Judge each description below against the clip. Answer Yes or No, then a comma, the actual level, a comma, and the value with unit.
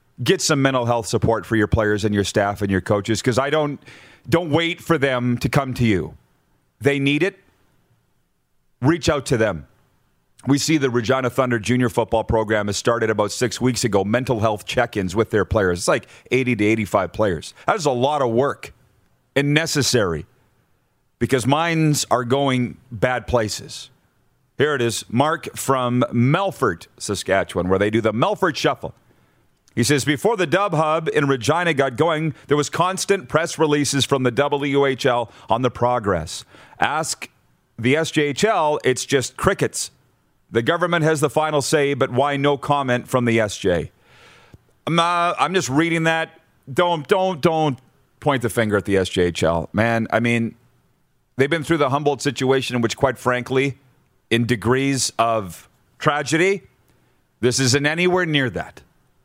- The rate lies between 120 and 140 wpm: No, average, 165 wpm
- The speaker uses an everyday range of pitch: Yes, average, 4.5 semitones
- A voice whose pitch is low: Yes, low, 130 Hz